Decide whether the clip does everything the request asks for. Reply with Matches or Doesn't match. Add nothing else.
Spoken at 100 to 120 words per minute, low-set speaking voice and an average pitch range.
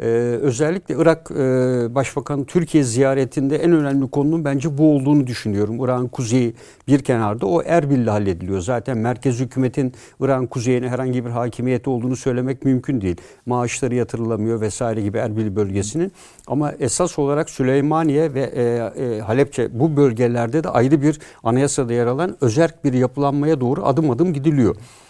Doesn't match